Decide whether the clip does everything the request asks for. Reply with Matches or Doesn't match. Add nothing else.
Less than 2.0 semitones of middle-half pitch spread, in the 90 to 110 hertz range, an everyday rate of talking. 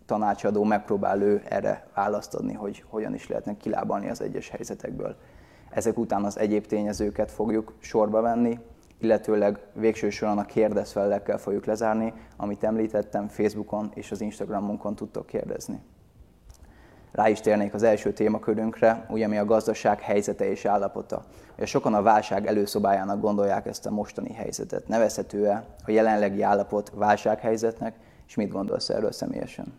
Matches